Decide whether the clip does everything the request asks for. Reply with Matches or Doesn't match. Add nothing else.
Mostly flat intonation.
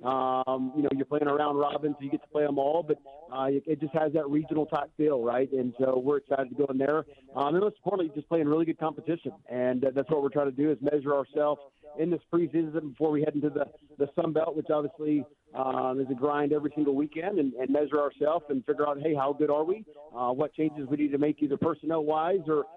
Matches